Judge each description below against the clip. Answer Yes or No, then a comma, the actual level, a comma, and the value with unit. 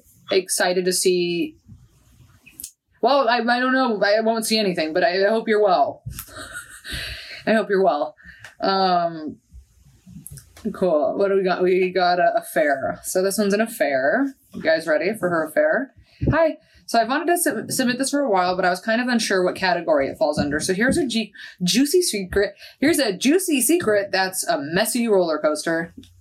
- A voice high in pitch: Yes, high, 215 Hz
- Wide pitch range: Yes, wide, 7.3 semitones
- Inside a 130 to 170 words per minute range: No, average, 185 wpm